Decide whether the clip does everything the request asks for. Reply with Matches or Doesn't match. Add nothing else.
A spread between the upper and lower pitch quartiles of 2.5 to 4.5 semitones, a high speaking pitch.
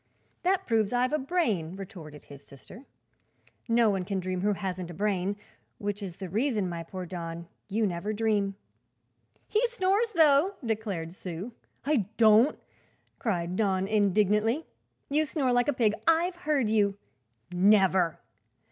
Doesn't match